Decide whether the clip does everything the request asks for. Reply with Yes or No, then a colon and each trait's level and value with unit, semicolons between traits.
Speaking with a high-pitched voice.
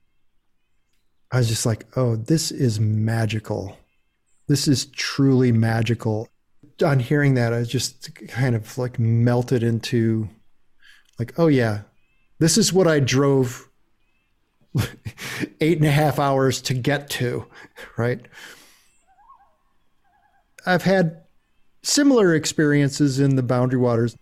No: low, 130 Hz